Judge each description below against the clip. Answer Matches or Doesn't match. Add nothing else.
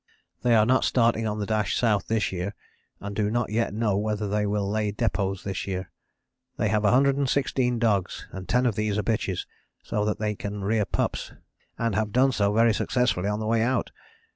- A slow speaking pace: Doesn't match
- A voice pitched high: Doesn't match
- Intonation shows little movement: Matches